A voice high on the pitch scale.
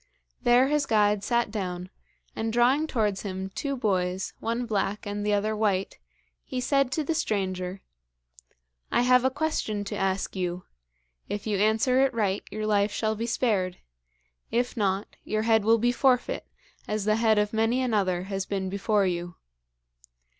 Yes: high, 215 Hz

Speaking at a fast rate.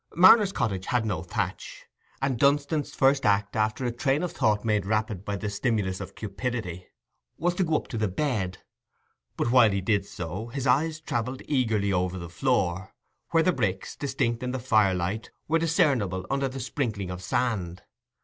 No: average, 180 wpm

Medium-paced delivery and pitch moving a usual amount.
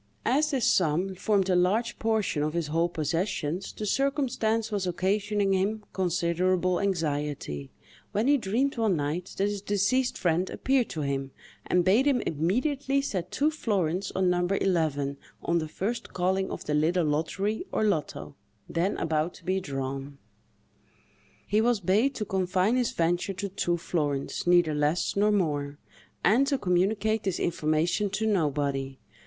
Yes: average, 155 wpm; average, 4.9 semitones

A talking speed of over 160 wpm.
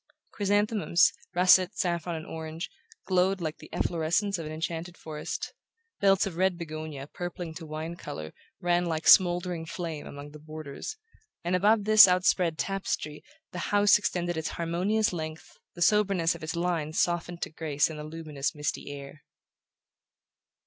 No: average, 150 wpm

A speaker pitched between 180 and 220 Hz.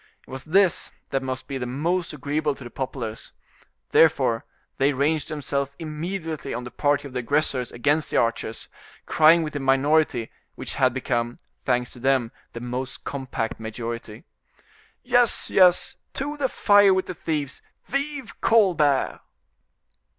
No: medium, 140 Hz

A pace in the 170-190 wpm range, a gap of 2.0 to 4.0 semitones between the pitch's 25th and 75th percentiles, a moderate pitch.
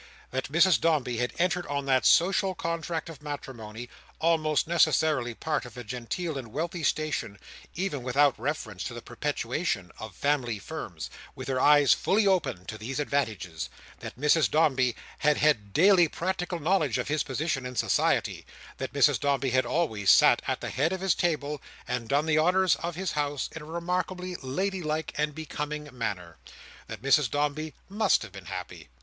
No: average, 175 wpm; average, 4.8 semitones; medium, 145 Hz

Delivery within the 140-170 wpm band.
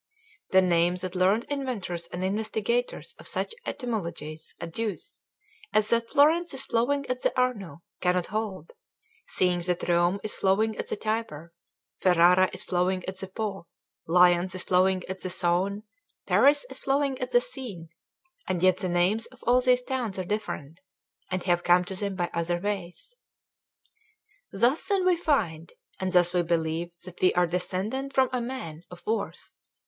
Yes: average, 165 wpm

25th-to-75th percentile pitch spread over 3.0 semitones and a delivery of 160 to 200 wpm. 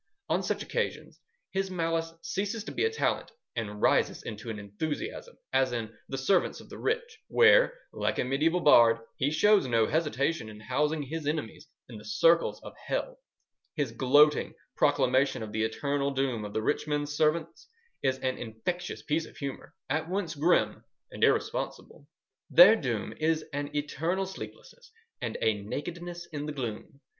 Yes: wide, 5.5 semitones; average, 165 wpm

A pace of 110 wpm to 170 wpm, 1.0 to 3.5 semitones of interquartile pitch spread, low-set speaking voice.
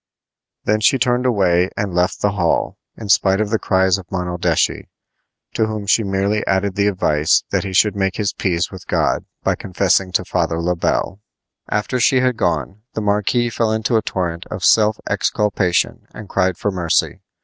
No: average, 180 wpm; average, 2.7 semitones; low, 100 Hz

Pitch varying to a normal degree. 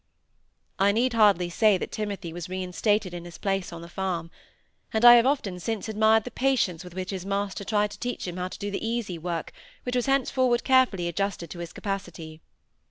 Yes: average, 4.1 semitones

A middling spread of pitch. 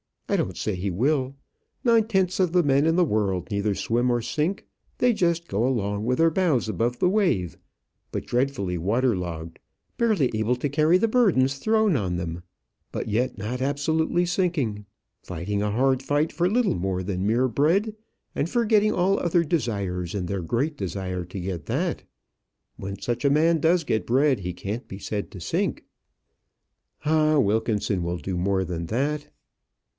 No: wide, 8.6 semitones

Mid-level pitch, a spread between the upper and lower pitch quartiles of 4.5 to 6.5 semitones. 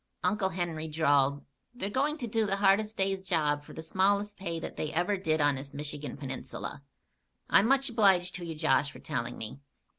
Yes: medium, 175 Hz; wide, 5.5 semitones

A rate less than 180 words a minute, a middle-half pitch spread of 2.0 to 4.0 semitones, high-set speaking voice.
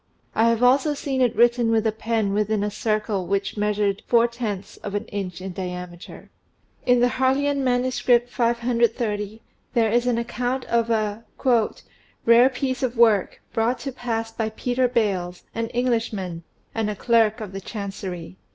Yes: average, 160 wpm; average, 3.0 semitones; high, 225 Hz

